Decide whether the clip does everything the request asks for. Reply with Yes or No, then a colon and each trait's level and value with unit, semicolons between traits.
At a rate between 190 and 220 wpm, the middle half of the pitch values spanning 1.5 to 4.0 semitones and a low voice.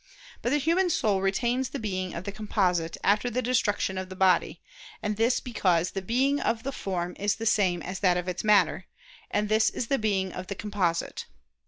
No: fast, 205 wpm; average, 3.7 semitones; high, 205 Hz